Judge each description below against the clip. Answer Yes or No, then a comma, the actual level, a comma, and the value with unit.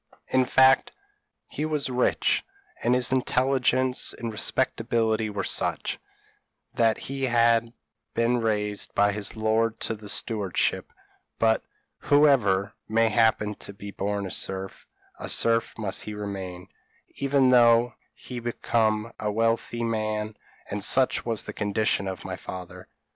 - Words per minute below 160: Yes, slow, 135 wpm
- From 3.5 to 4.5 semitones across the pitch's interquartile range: No, average, 2.7 semitones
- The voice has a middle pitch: No, low, 115 Hz